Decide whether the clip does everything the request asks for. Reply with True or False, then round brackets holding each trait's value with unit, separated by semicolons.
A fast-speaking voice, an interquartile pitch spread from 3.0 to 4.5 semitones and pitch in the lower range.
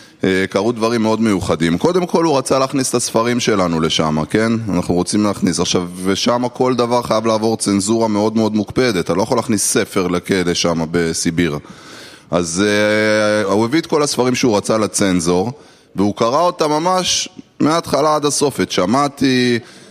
False (160 wpm; 5.1 semitones; 110 Hz)